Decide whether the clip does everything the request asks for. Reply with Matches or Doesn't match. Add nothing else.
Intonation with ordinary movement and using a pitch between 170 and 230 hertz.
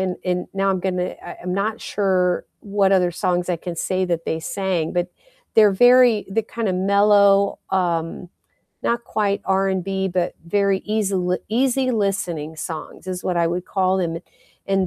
Doesn't match